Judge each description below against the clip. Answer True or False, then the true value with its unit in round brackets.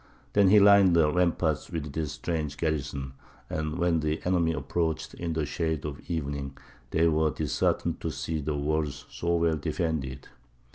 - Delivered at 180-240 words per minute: False (160 wpm)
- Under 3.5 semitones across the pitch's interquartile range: True (2.4 semitones)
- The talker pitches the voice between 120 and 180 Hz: False (80 Hz)